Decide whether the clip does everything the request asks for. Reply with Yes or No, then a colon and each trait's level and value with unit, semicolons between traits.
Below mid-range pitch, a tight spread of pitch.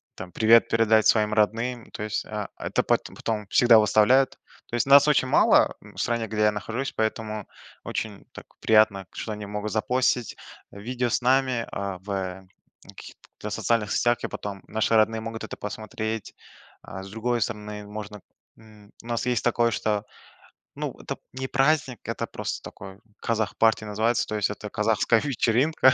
Yes: low, 110 Hz; narrow, 2.2 semitones